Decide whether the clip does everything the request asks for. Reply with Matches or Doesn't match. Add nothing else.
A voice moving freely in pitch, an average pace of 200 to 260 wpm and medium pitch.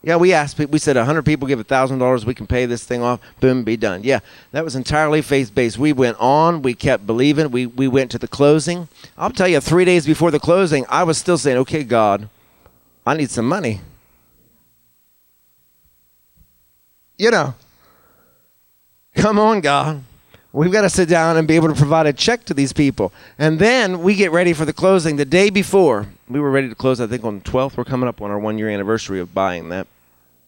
Doesn't match